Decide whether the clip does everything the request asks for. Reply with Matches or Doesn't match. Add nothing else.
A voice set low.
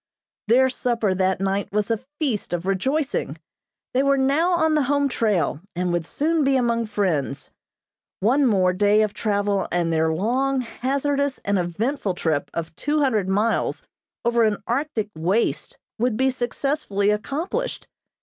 Doesn't match